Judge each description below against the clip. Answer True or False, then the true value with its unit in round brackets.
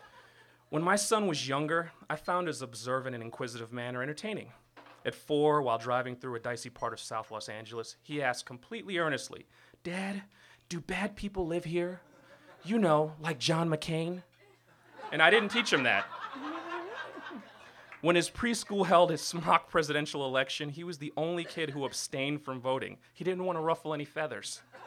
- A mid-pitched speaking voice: True (155 Hz)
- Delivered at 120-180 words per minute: True (170 wpm)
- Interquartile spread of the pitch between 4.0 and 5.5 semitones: True (5.1 semitones)